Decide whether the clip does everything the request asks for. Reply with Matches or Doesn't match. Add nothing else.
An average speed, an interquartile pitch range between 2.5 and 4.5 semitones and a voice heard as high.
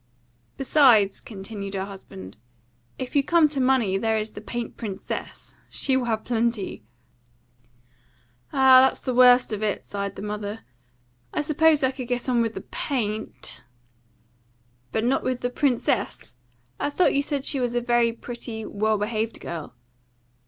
Matches